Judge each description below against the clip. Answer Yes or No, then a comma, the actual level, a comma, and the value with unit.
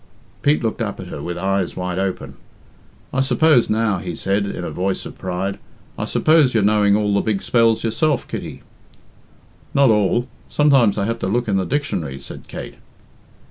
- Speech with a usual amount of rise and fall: Yes, average, 4.2 semitones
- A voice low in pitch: Yes, low, 105 Hz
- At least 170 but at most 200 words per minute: Yes, average, 180 wpm